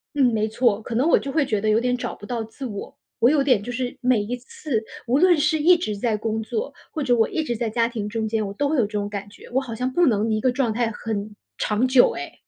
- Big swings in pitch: No, average, 3.5 semitones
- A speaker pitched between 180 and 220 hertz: No, high, 235 Hz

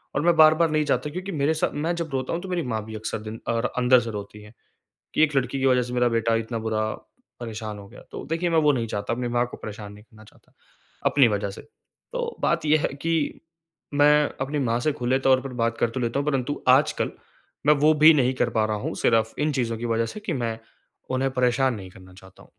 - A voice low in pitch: Yes, low, 125 Hz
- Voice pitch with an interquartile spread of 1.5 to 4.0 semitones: No, average, 4.8 semitones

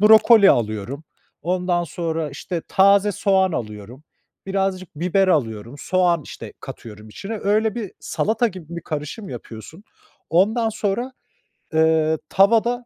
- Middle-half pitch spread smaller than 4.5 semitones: No, average, 5.0 semitones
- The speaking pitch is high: No, medium, 180 Hz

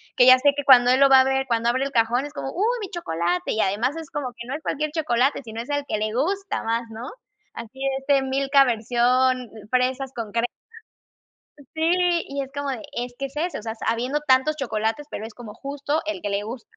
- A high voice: Yes, very high, 260 Hz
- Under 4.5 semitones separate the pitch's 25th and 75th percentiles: Yes, average, 3.5 semitones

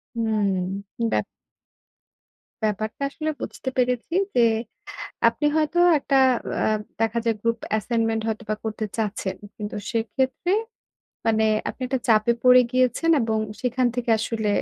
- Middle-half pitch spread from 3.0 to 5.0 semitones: No, narrow, 2.6 semitones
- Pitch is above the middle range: Yes, high, 230 Hz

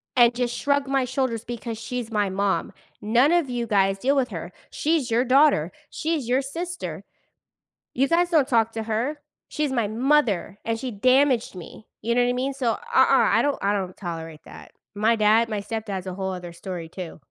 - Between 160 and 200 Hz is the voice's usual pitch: No, high, 235 Hz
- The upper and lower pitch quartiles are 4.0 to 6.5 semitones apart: Yes, average, 4.8 semitones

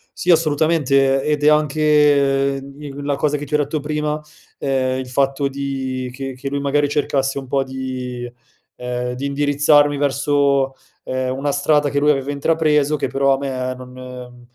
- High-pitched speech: No, medium, 140 Hz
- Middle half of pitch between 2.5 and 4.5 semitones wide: No, narrow, 1.8 semitones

